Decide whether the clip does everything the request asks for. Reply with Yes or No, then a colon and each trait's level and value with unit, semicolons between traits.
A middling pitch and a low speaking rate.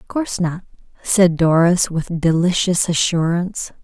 Yes: medium, 175 Hz; slow, 125 wpm